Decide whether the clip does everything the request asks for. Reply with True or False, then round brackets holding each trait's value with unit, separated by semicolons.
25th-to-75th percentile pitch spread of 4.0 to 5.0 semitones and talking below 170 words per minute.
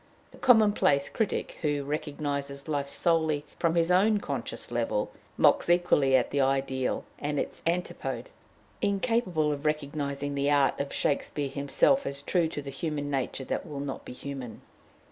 False (3.3 semitones; 155 wpm)